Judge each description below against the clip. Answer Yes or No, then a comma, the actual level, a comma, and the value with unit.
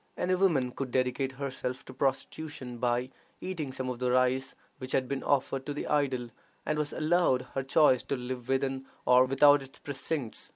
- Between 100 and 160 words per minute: No, average, 180 wpm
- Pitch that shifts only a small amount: Yes, narrow, 2.1 semitones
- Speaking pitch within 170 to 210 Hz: No, low, 135 Hz